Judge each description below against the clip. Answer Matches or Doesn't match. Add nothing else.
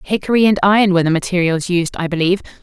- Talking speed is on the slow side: Doesn't match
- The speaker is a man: Doesn't match